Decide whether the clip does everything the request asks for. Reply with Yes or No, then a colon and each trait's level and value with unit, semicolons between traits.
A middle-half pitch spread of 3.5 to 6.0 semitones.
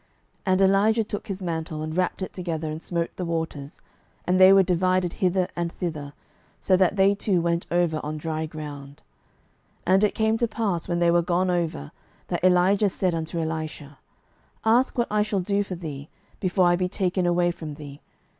No: average, 2.9 semitones